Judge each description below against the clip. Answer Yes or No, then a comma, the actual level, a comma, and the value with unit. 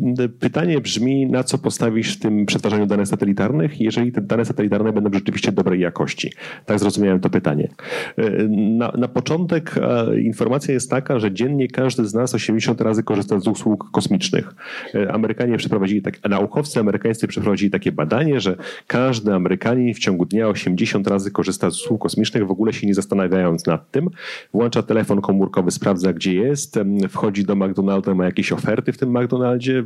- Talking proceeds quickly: Yes, fast, 165 wpm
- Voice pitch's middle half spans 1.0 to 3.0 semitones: No, average, 3.6 semitones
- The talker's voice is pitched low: Yes, low, 110 Hz